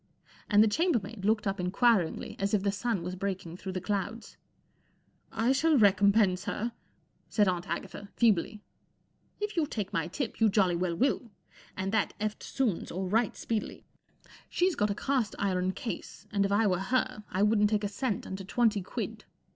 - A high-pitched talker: Yes, high, 205 Hz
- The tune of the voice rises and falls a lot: No, average, 3.2 semitones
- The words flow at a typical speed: Yes, average, 180 wpm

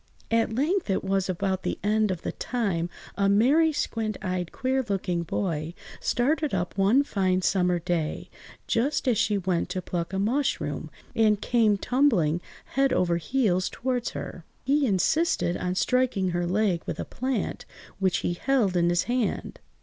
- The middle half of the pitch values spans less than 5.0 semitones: No, wide, 5.6 semitones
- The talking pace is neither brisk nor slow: Yes, average, 155 wpm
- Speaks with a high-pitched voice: Yes, high, 200 Hz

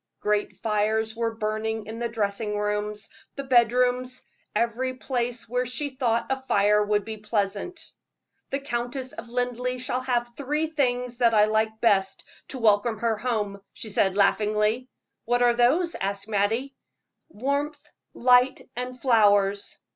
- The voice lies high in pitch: Yes, high, 235 Hz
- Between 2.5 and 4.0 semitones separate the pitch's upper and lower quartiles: Yes, average, 3.0 semitones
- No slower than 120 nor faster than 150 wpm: Yes, average, 145 wpm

